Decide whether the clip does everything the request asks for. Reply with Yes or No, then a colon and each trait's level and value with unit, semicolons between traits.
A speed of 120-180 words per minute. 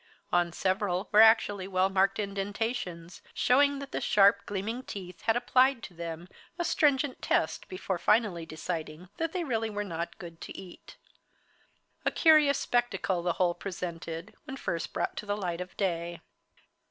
Yes: average, 155 wpm